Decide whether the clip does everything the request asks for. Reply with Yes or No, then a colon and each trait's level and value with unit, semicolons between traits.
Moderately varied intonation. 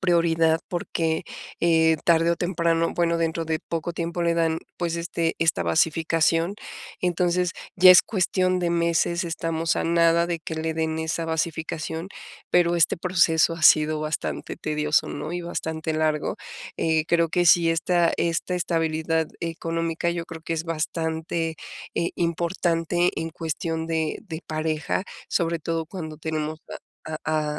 No: narrow, 1.1 semitones